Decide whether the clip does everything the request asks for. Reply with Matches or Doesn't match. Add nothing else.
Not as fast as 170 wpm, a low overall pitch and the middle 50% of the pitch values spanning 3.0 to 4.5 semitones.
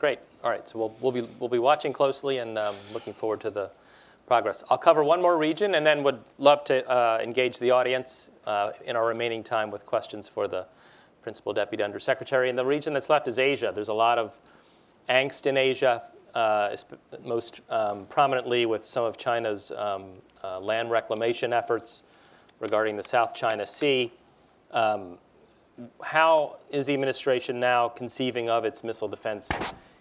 Doesn't match